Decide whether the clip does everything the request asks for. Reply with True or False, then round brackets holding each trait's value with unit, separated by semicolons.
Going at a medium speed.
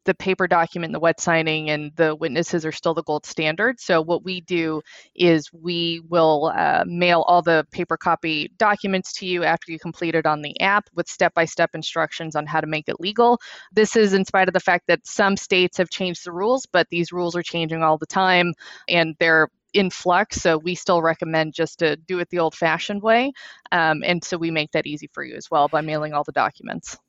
False (225 wpm)